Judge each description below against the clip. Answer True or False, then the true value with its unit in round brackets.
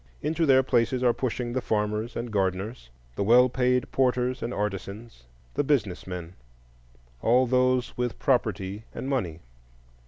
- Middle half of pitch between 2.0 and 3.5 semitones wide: False (5.2 semitones)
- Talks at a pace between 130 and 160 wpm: True (135 wpm)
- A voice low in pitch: True (115 Hz)